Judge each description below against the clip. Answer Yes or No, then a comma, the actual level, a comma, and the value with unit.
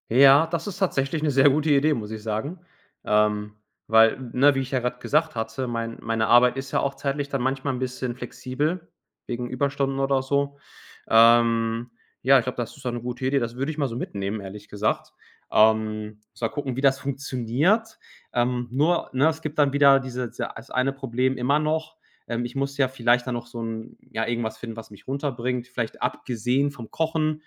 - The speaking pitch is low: Yes, low, 130 Hz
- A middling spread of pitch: Yes, average, 3.2 semitones